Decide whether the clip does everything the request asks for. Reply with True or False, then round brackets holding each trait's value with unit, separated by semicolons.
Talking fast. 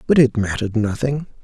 False (165 wpm)